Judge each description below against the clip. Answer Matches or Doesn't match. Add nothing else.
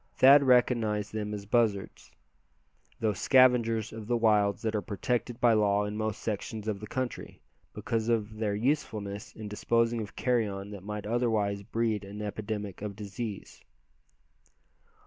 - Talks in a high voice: Doesn't match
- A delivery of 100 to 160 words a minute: Matches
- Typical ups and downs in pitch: Doesn't match